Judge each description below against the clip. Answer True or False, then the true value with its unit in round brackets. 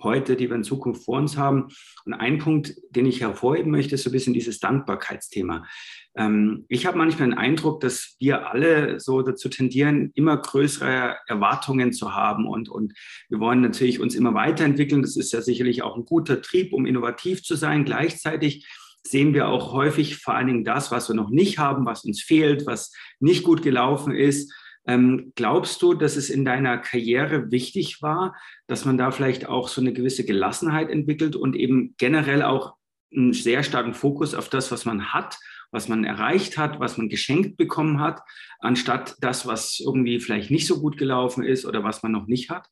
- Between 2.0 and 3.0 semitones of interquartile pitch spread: False (3.6 semitones)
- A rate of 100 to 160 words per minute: False (190 wpm)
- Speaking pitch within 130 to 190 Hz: True (135 Hz)